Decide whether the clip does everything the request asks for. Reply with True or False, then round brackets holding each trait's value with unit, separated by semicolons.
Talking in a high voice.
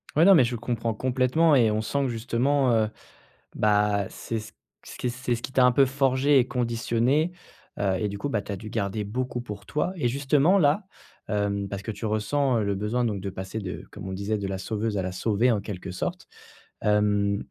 False (115 Hz)